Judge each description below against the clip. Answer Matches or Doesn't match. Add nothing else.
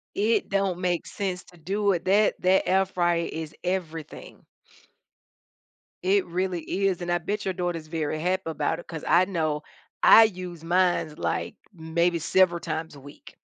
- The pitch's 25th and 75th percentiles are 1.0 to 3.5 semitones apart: Matches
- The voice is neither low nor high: Matches